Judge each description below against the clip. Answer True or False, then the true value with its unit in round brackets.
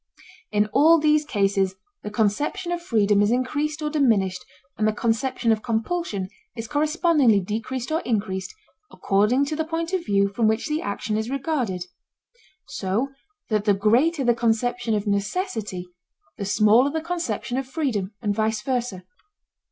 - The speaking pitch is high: True (230 Hz)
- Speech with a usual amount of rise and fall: False (6.2 semitones)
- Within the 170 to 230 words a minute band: False (155 wpm)